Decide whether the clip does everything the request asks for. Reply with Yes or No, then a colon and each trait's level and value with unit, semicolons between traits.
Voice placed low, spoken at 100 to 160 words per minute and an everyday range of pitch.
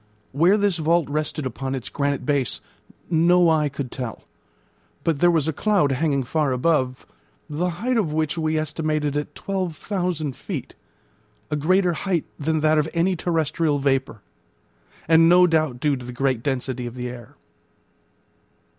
No: medium, 155 Hz; average, 155 wpm; average, 3.5 semitones